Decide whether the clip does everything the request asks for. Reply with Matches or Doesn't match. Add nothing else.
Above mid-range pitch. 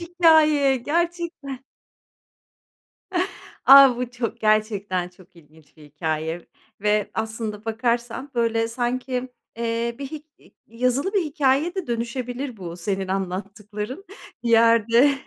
Matches